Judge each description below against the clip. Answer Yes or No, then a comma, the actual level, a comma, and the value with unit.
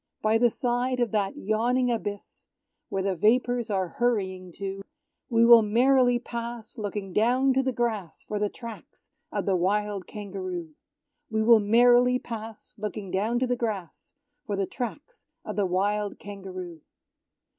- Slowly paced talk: No, average, 155 wpm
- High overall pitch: Yes, high, 215 Hz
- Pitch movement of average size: Yes, average, 3.6 semitones